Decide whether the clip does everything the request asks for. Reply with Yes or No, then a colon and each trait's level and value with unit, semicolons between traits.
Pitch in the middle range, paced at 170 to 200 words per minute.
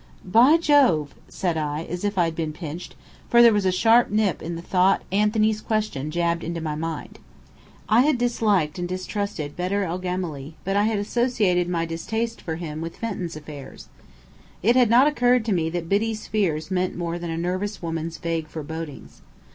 Yes: medium, 180 Hz; average, 185 wpm